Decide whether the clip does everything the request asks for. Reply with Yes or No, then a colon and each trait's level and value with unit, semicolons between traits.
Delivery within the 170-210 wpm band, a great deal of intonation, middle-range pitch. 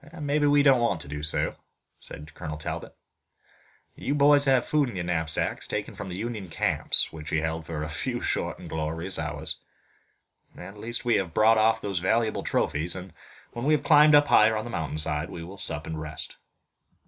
No: average, 195 wpm; wide, 7.0 semitones; very low, 95 Hz